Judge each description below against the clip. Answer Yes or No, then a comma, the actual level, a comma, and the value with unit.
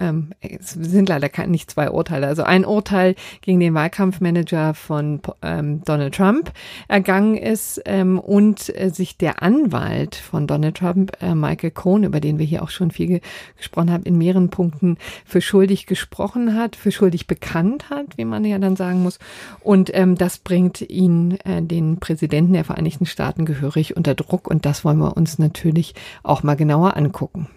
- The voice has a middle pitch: Yes, medium, 175 Hz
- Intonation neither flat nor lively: Yes, average, 3.1 semitones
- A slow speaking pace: No, average, 160 wpm